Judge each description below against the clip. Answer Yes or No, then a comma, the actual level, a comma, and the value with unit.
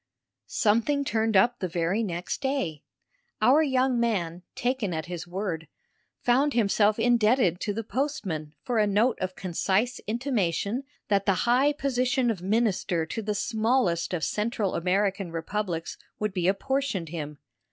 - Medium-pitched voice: No, high, 210 Hz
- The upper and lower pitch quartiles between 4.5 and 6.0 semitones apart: Yes, average, 5.3 semitones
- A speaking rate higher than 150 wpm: No, average, 145 wpm